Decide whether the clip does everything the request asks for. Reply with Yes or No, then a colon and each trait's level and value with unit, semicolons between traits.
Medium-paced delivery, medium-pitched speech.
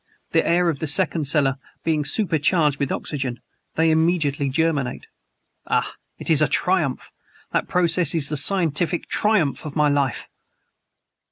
Yes: average, 150 wpm; medium, 155 Hz